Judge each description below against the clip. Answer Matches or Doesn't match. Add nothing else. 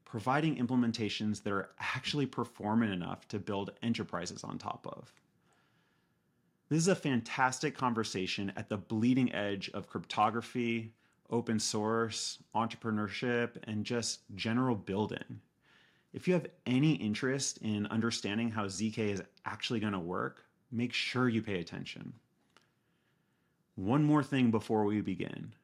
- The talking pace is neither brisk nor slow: Doesn't match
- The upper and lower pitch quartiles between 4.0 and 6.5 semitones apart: Doesn't match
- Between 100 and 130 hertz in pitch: Matches